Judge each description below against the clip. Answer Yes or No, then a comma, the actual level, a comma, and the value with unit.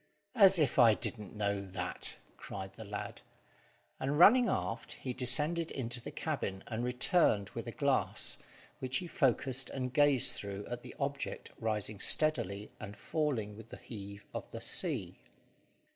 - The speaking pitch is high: No, low, 120 Hz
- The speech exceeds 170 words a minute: No, average, 155 wpm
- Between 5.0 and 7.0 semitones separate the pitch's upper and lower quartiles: Yes, wide, 5.5 semitones